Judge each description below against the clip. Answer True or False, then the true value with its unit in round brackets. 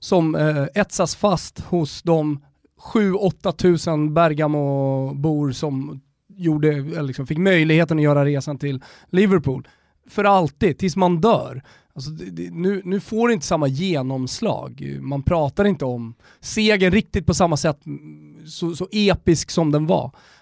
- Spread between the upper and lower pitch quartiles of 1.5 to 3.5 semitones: False (4.8 semitones)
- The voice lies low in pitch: False (160 Hz)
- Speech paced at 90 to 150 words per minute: True (145 wpm)